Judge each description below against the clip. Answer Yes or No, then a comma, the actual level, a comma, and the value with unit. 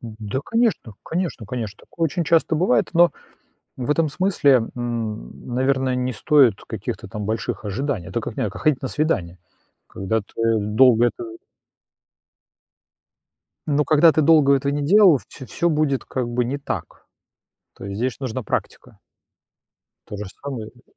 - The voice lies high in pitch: No, low, 130 Hz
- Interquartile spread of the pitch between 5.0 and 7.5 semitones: Yes, average, 5.3 semitones